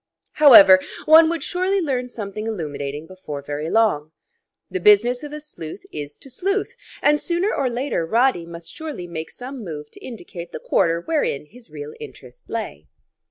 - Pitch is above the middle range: Yes, high, 225 Hz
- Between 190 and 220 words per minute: No, average, 165 wpm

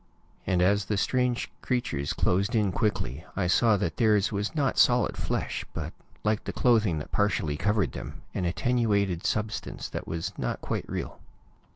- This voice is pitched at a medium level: No, low, 105 Hz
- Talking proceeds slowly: No, average, 165 wpm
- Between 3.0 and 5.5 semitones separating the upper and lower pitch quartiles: Yes, average, 4.0 semitones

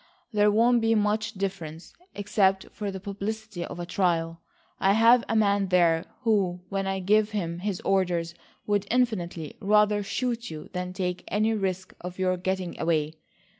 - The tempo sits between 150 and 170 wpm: Yes, average, 160 wpm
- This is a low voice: No, high, 195 Hz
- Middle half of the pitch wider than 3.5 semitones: No, average, 2.9 semitones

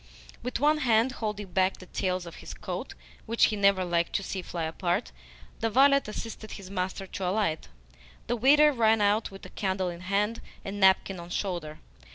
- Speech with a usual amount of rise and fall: Yes, average, 3.5 semitones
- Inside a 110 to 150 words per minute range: No, average, 185 wpm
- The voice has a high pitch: Yes, high, 200 Hz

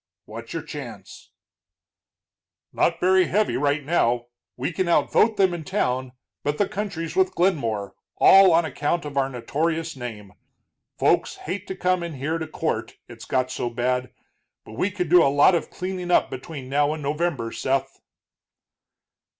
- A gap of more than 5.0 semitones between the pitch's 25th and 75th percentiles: Yes, wide, 5.6 semitones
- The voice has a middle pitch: Yes, medium, 155 Hz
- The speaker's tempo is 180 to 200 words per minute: No, average, 165 wpm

